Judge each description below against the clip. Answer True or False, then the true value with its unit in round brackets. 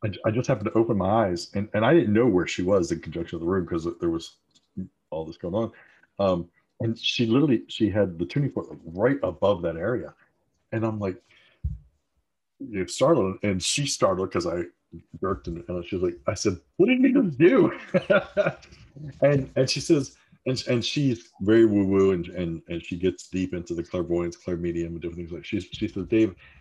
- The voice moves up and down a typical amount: False (6.8 semitones)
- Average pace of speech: False (210 wpm)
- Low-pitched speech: True (100 Hz)